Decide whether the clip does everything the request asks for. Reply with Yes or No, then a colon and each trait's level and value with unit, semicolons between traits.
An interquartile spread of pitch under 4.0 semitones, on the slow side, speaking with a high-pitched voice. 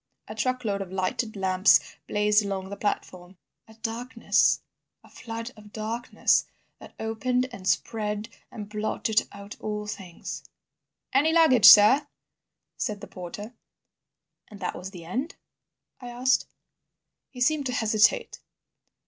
Yes: average, 3.3 semitones; slow, 130 wpm; high, 215 Hz